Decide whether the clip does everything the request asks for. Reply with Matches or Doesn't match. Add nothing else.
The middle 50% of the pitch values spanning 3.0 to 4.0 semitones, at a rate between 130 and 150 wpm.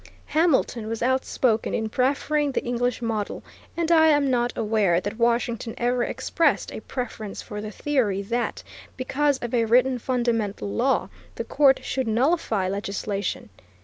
Matches